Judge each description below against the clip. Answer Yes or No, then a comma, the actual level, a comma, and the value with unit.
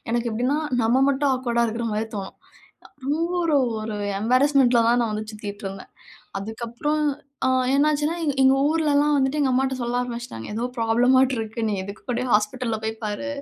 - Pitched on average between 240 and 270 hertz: Yes, high, 245 Hz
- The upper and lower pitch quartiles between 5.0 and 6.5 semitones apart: No, average, 3.7 semitones